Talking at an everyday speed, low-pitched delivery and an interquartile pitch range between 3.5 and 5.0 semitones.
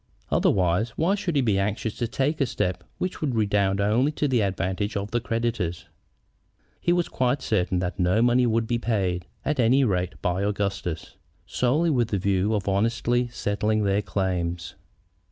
Yes: average, 170 wpm; low, 105 Hz; average, 4.3 semitones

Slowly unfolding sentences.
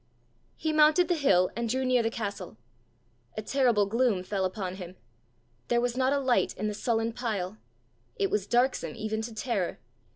No: average, 175 wpm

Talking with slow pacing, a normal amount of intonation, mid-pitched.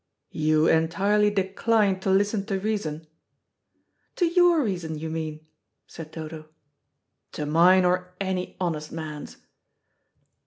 Yes: slow, 115 wpm; average, 4.1 semitones; medium, 180 Hz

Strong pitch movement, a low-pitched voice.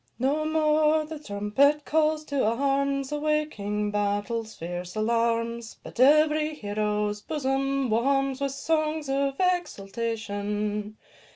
No: wide, 6.3 semitones; very high, 270 Hz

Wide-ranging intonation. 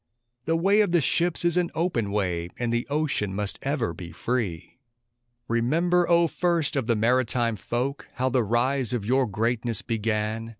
Yes: wide, 6.2 semitones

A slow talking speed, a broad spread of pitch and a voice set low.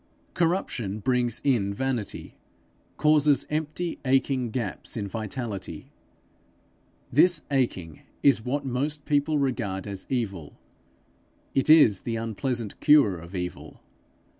Yes: slow, 110 wpm; wide, 5.7 semitones; low, 125 Hz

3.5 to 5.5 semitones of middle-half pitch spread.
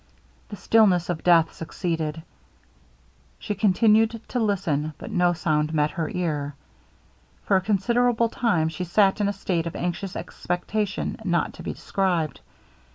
Yes: average, 4.2 semitones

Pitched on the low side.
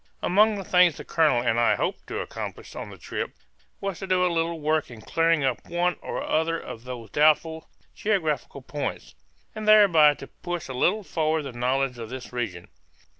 No: medium, 155 Hz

